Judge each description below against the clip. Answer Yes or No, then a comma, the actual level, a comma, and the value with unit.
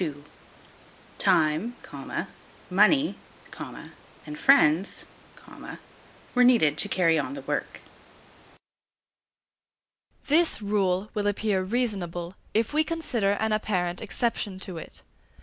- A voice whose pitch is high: Yes, high, 205 Hz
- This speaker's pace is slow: Yes, slow, 95 wpm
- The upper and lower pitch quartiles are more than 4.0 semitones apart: Yes, average, 5.1 semitones